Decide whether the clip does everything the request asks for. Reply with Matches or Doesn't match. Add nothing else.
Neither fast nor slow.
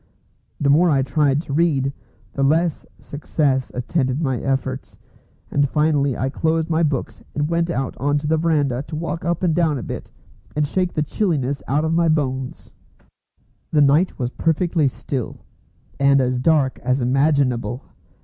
Matches